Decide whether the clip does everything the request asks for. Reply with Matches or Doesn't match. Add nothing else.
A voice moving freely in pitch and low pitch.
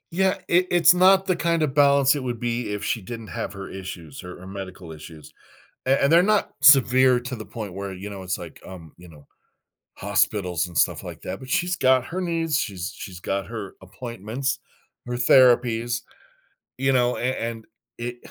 Matches